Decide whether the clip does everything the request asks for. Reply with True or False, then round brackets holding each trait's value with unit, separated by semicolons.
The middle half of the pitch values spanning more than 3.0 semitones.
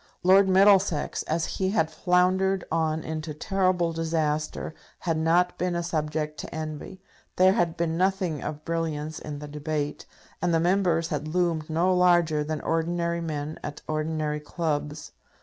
False (2.6 semitones)